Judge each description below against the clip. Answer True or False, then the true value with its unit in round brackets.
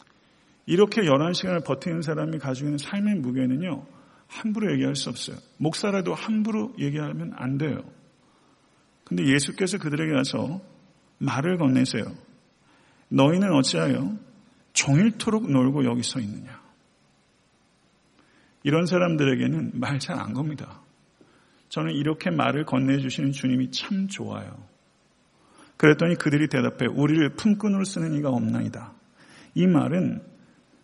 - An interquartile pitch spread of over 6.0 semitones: False (5.5 semitones)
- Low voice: False (150 Hz)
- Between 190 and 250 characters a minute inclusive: False (280 characters per minute)